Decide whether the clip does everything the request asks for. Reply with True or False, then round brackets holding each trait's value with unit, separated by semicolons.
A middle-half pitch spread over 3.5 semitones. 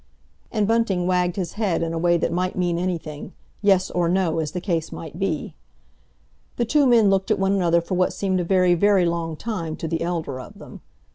False (2.5 semitones)